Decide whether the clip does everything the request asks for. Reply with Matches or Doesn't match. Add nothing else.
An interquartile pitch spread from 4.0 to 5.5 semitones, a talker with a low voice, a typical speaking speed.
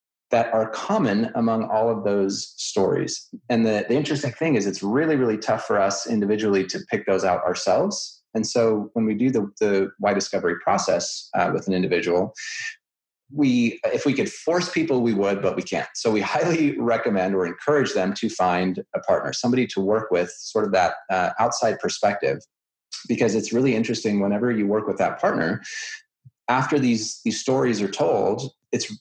Matches